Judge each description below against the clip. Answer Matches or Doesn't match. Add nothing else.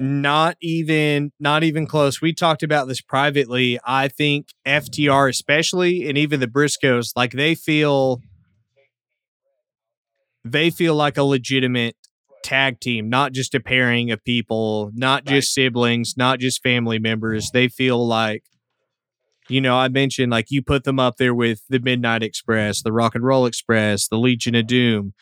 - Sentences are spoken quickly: Doesn't match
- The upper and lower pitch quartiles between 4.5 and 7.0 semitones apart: Doesn't match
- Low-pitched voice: Matches